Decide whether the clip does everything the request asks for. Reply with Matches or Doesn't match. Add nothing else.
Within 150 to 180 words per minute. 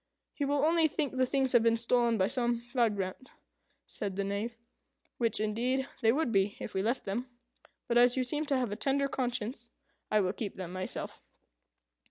Doesn't match